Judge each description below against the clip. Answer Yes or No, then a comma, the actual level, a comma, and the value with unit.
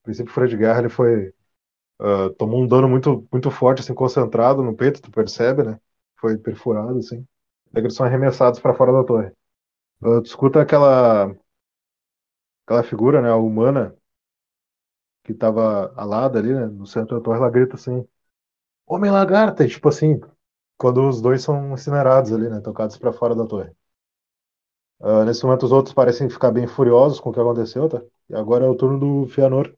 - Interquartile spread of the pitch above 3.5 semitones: No, average, 3.1 semitones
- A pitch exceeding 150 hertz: No, low, 120 Hz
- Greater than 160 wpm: Yes, average, 175 wpm